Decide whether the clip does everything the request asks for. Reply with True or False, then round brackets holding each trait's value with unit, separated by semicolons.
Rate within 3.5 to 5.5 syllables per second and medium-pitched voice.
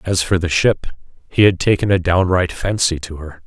False (5.0 syllables/s; 90 Hz)